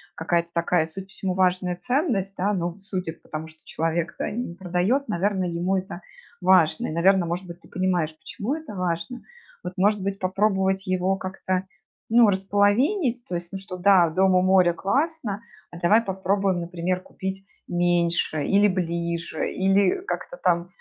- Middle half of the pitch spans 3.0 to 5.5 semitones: No, narrow, 2.4 semitones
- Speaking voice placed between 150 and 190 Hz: Yes, medium, 185 Hz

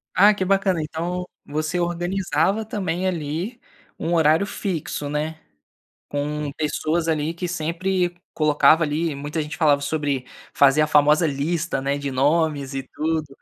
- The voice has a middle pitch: Yes, medium, 160 Hz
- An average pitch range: Yes, average, 3.1 semitones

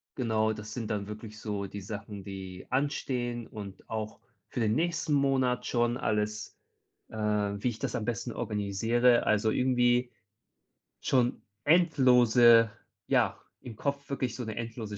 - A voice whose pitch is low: Yes, low, 115 Hz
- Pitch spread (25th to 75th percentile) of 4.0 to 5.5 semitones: No, average, 2.7 semitones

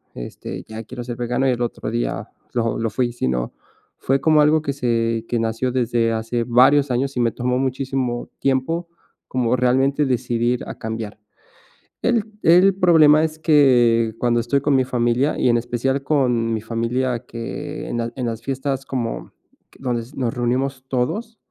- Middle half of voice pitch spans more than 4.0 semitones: No, narrow, 2.6 semitones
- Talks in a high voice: No, low, 125 Hz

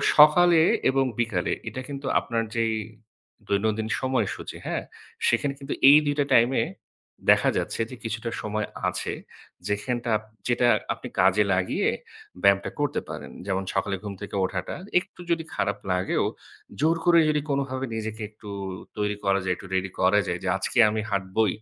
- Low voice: Yes, low, 110 Hz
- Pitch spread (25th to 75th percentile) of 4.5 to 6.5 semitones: Yes, average, 5.0 semitones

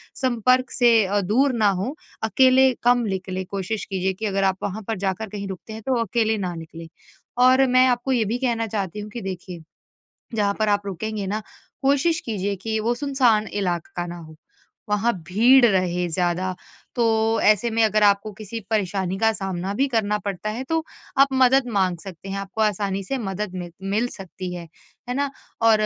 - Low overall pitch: No, high, 210 Hz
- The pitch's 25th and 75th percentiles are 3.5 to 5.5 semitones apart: Yes, average, 3.8 semitones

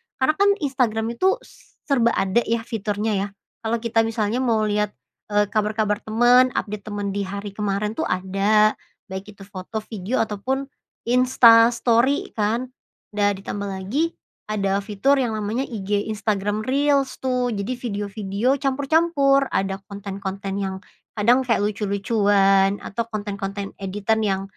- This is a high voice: Yes, high, 215 Hz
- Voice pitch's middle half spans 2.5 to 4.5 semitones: Yes, average, 3.3 semitones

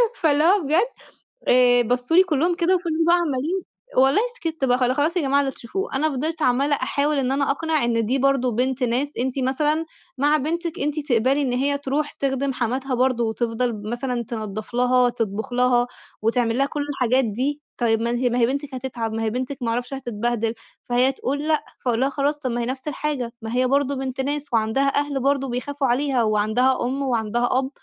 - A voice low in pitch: No, very high, 260 Hz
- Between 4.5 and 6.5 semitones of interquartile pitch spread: No, average, 3.0 semitones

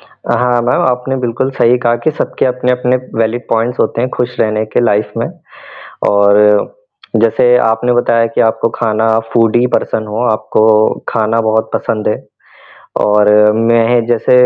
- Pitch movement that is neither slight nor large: No, narrow, 1.9 semitones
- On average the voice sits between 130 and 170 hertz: No, low, 115 Hz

